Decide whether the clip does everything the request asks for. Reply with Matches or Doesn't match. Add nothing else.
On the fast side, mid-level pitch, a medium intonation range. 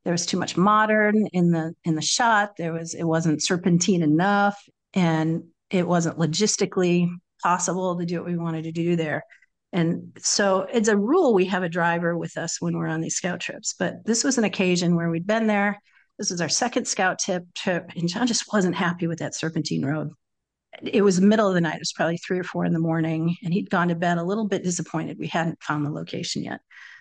Matches